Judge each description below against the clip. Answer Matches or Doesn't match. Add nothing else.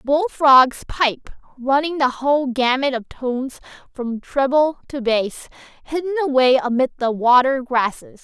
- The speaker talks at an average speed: Doesn't match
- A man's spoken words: Doesn't match